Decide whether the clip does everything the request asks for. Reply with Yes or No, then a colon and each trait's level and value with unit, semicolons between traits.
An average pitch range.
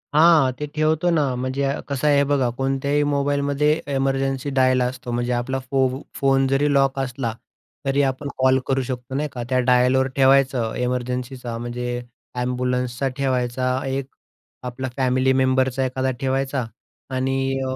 No: narrow, 1.4 semitones